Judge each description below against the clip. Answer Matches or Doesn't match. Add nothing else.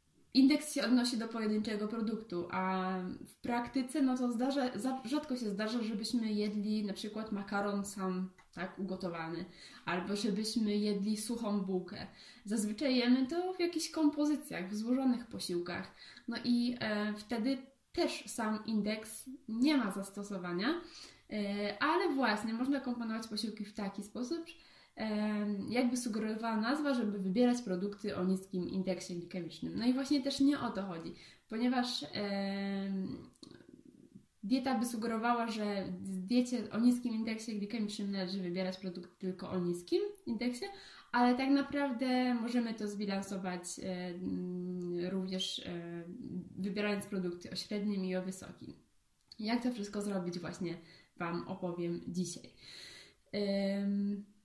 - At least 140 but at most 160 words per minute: Doesn't match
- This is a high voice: Matches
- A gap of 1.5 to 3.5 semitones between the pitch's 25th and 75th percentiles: Doesn't match